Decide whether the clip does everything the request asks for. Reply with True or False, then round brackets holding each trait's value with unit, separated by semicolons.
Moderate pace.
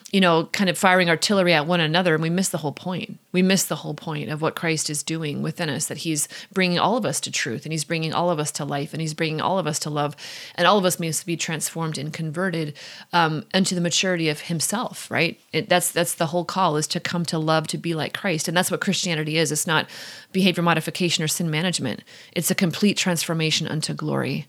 False (245 wpm)